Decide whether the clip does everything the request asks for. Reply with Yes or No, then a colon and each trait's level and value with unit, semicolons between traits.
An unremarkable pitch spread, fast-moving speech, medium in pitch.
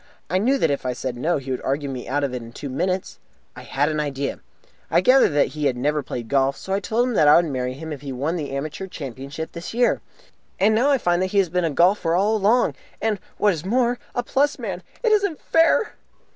No: wide, 7.3 semitones; fast, 250 wpm; medium, 165 Hz